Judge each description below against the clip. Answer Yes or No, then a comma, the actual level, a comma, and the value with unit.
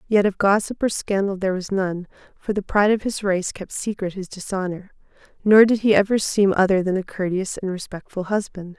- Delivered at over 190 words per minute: Yes, fast, 205 wpm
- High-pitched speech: Yes, high, 195 Hz